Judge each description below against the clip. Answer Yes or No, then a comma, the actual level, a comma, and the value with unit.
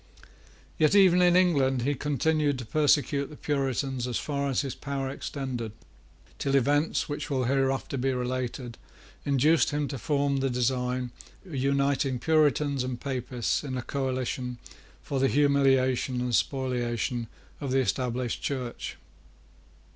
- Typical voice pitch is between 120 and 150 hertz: Yes, low, 135 Hz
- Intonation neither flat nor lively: No, narrow, 2.2 semitones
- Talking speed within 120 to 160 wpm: Yes, average, 140 wpm